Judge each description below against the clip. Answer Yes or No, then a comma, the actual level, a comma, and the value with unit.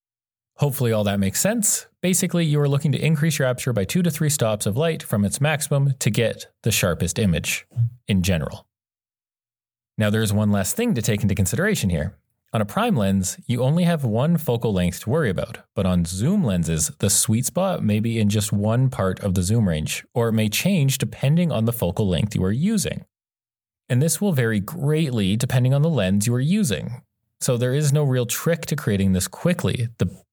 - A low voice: Yes, low, 115 Hz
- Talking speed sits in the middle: No, fast, 210 wpm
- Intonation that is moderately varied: No, wide, 6.4 semitones